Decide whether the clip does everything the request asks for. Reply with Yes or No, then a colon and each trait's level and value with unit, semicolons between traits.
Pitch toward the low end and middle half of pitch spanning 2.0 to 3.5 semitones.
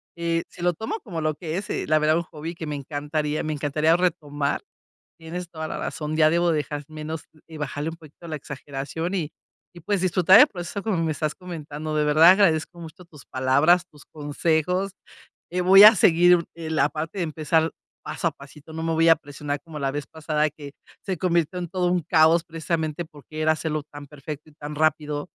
No: medium, 160 Hz; narrow, 2.4 semitones